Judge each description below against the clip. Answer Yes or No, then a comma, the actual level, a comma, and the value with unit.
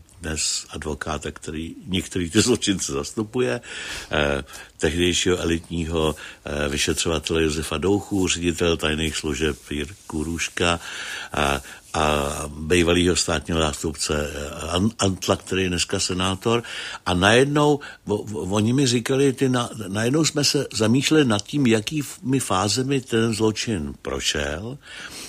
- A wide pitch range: Yes, wide, 6.0 semitones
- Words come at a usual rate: No, slow, 110 wpm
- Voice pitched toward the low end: Yes, very low, 90 Hz